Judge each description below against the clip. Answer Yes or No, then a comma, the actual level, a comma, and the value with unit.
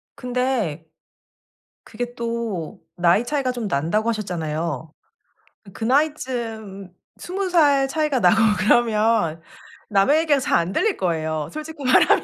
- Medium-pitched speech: No, high, 230 Hz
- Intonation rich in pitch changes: Yes, wide, 7.2 semitones